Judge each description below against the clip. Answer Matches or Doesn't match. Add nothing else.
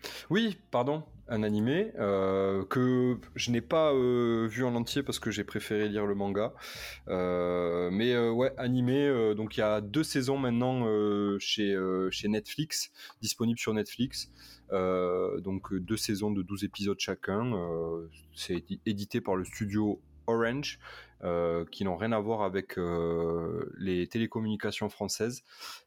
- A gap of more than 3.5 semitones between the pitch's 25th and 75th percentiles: Matches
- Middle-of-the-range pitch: Doesn't match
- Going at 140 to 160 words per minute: Matches